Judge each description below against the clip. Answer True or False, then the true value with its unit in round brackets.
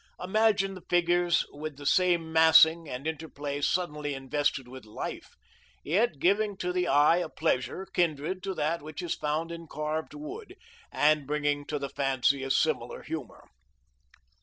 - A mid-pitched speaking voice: True (160 Hz)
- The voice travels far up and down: False (3.6 semitones)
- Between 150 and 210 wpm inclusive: True (155 wpm)